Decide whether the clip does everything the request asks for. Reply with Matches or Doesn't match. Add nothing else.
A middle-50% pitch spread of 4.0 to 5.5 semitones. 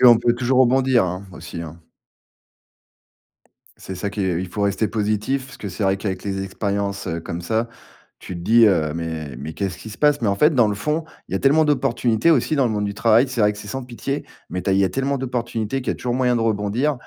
Matches